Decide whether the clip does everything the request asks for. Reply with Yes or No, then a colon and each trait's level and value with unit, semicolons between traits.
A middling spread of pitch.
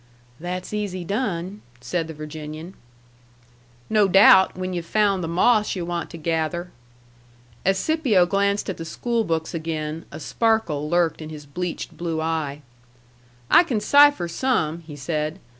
Yes: average, 4.0 semitones